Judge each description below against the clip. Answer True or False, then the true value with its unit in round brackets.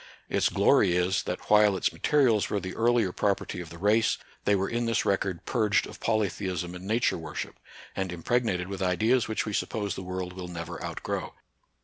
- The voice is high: False (95 Hz)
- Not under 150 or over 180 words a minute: False (190 wpm)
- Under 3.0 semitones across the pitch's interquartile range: False (3.3 semitones)